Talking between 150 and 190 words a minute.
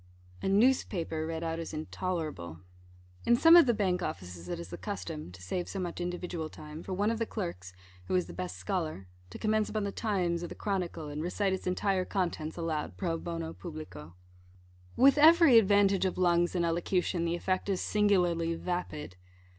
Yes: average, 185 wpm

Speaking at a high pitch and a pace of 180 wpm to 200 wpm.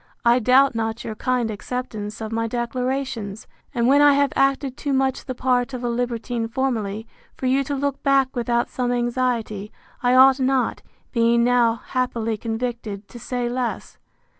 No: high, 245 Hz; average, 165 wpm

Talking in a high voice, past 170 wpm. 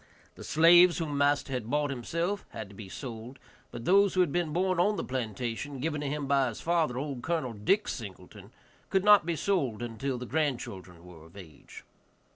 No: medium, 140 Hz; average, 195 wpm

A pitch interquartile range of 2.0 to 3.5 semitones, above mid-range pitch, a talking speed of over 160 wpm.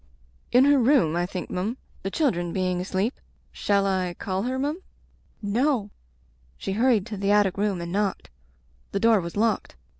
No: average, 4.0 semitones; high, 200 Hz; average, 175 wpm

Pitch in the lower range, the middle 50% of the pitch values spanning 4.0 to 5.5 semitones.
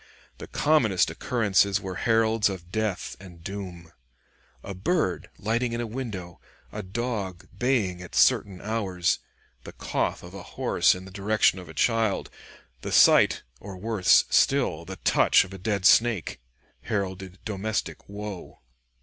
No: low, 100 Hz; average, 3.3 semitones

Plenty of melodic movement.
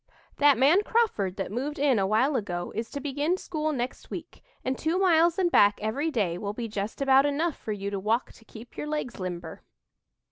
Yes: wide, 6.4 semitones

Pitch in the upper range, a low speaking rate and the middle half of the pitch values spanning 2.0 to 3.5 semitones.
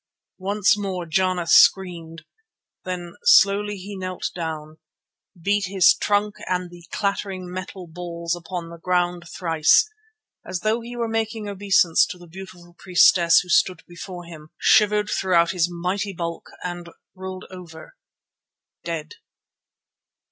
No: medium, 180 Hz; slow, 125 wpm; narrow, 2.5 semitones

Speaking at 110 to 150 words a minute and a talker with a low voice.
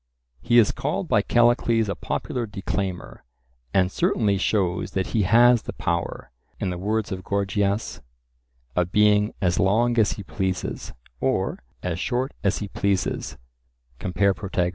Yes: average, 145 wpm; low, 100 Hz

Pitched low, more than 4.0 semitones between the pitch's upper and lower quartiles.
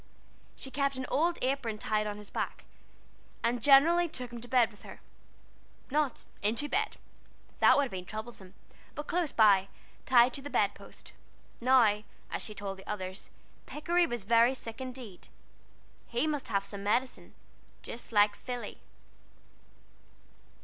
No: high, 240 Hz; average, 4.7 semitones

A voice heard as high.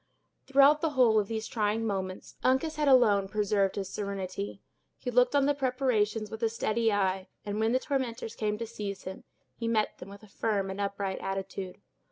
Yes: high, 215 Hz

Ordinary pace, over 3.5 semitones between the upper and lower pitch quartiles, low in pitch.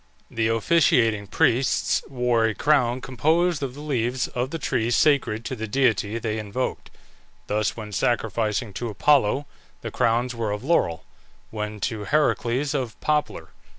Yes: average, 150 wpm; average, 4.0 semitones; low, 120 Hz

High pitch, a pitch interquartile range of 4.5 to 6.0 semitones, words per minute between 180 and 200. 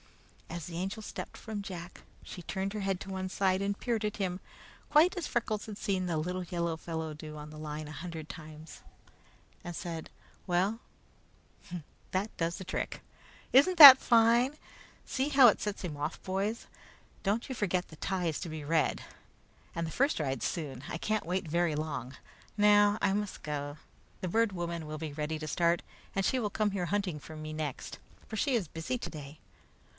No: medium, 180 Hz; average, 4.8 semitones; average, 190 wpm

